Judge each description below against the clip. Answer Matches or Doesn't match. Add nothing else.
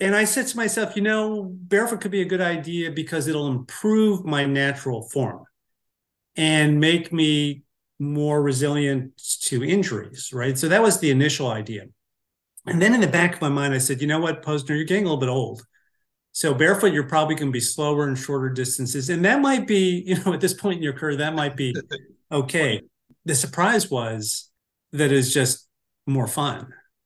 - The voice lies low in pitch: Doesn't match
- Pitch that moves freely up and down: Doesn't match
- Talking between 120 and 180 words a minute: Doesn't match